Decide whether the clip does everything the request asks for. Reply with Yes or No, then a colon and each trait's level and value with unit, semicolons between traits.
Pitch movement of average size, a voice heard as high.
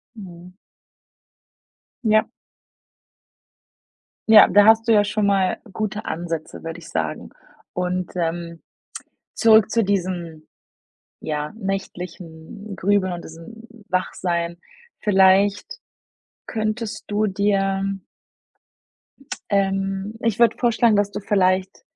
Yes: average, 3.1 semitones; high, 195 Hz